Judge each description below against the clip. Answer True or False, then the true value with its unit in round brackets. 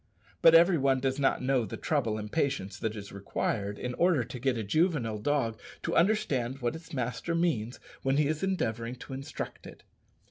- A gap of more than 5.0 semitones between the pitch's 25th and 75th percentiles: True (5.5 semitones)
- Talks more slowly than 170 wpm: False (190 wpm)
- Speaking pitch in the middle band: False (130 Hz)